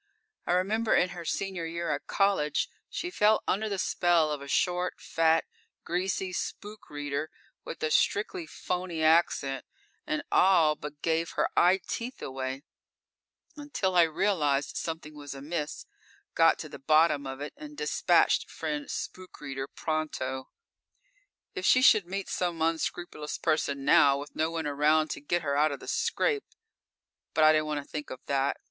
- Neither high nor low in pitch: Yes, medium, 160 Hz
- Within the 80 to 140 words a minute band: No, average, 165 wpm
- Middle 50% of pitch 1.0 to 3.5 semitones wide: No, average, 4.1 semitones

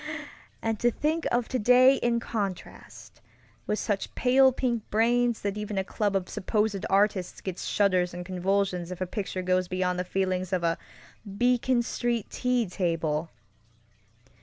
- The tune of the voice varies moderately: Yes, average, 4.6 semitones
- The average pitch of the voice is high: Yes, high, 200 Hz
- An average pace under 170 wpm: Yes, average, 150 wpm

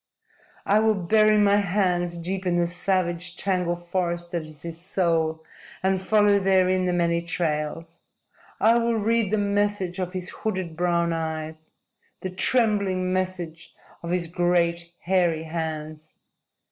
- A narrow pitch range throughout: Yes, narrow, 2.3 semitones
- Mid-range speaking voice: Yes, medium, 180 Hz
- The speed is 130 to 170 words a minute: Yes, average, 140 wpm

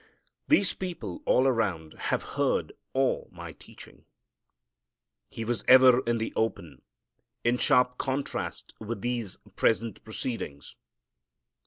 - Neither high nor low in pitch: No, low, 120 Hz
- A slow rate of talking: Yes, slow, 115 wpm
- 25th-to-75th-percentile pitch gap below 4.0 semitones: Yes, average, 2.8 semitones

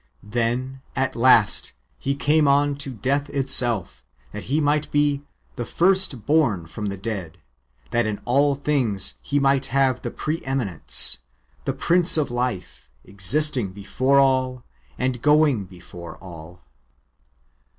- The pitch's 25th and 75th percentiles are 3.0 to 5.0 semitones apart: No, wide, 5.6 semitones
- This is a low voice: Yes, low, 130 Hz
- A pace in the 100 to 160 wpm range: Yes, average, 140 wpm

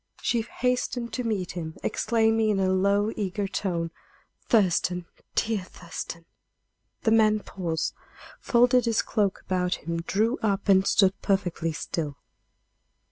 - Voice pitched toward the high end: Yes, high, 200 Hz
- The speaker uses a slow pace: Yes, slow, 130 wpm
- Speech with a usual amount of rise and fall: Yes, average, 3.8 semitones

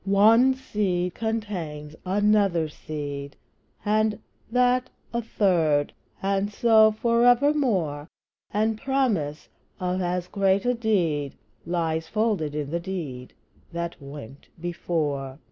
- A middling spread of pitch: No, wide, 6.0 semitones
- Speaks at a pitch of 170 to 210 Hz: Yes, high, 190 Hz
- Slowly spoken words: Yes, slow, 110 wpm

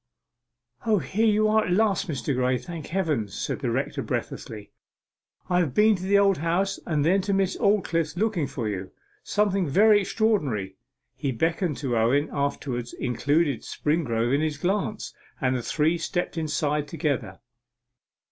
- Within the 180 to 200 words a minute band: No, average, 155 wpm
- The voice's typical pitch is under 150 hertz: No, medium, 160 Hz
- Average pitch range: No, wide, 6.1 semitones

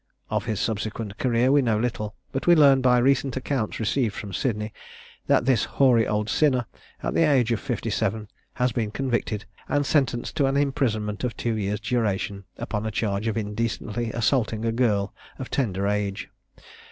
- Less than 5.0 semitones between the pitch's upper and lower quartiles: Yes, average, 3.5 semitones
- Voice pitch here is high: No, low, 115 Hz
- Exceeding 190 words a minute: No, average, 175 wpm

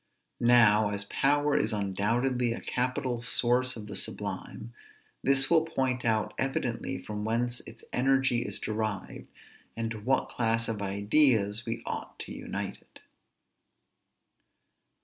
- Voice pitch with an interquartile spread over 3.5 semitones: No, average, 3.0 semitones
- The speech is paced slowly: Yes, slow, 130 wpm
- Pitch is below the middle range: Yes, low, 120 Hz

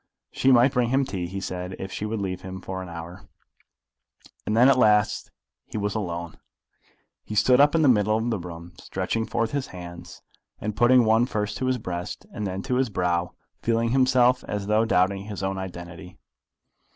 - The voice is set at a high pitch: No, low, 105 Hz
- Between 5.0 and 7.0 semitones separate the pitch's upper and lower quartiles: No, average, 4.6 semitones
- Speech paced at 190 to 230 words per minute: Yes, average, 195 wpm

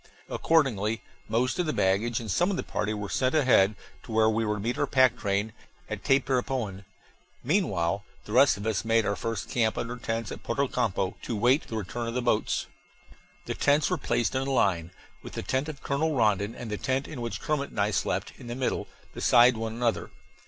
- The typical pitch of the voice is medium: No, low, 115 Hz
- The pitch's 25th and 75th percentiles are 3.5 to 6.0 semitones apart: Yes, average, 3.8 semitones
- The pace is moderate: No, fast, 215 wpm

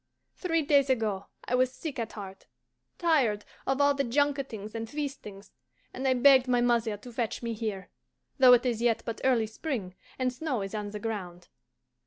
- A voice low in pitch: No, high, 240 Hz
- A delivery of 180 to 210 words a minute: Yes, average, 185 wpm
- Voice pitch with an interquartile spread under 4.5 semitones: Yes, average, 3.9 semitones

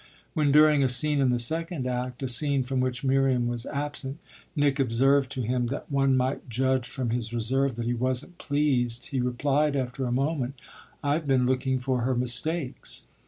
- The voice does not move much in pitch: Yes, narrow, 2.3 semitones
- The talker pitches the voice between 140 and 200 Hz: No, low, 130 Hz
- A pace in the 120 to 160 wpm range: No, average, 185 wpm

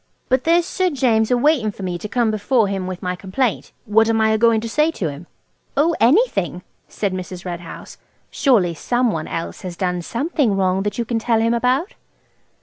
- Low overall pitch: No, high, 220 Hz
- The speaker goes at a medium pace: No, fast, 210 wpm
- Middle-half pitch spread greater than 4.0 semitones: Yes, average, 5.3 semitones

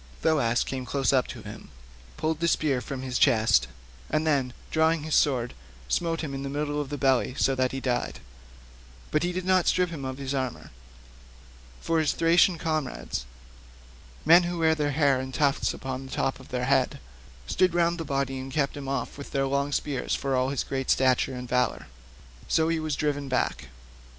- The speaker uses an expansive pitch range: No, average, 3.2 semitones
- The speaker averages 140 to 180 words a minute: No, average, 200 wpm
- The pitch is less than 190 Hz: Yes, medium, 140 Hz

